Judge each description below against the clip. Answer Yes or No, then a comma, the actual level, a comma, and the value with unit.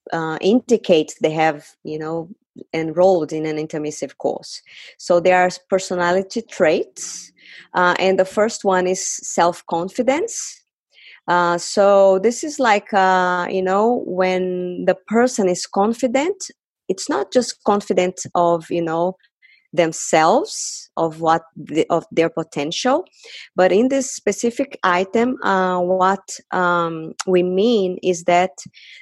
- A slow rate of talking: Yes, slow, 130 wpm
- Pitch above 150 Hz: Yes, medium, 185 Hz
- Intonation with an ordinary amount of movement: Yes, average, 4.0 semitones